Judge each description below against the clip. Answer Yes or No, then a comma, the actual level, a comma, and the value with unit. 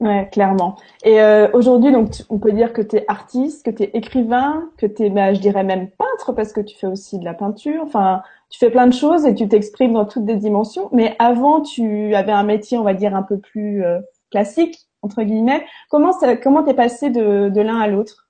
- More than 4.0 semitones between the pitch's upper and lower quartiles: No, average, 3.7 semitones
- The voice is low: No, high, 220 Hz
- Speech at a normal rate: No, fast, 240 wpm